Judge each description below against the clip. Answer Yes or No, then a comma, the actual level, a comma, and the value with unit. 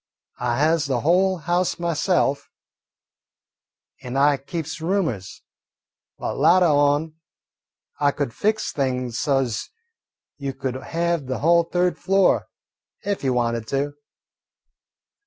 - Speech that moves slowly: Yes, slow, 120 wpm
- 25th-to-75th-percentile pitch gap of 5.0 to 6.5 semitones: No, average, 4.4 semitones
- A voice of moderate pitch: Yes, medium, 145 Hz